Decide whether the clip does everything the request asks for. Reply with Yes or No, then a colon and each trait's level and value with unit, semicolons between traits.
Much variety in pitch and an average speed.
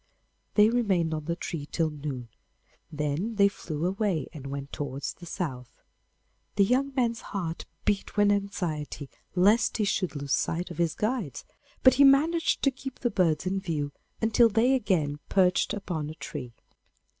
Yes: wide, 6.2 semitones; average, 165 wpm